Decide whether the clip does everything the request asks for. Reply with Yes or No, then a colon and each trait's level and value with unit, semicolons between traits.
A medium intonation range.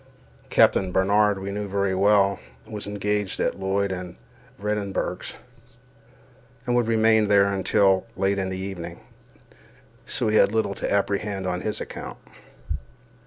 No: narrow, 1.4 semitones